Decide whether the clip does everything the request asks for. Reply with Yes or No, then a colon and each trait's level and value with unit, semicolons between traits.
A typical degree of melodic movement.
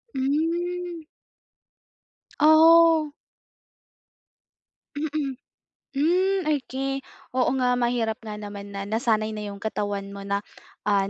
No: wide, 6.9 semitones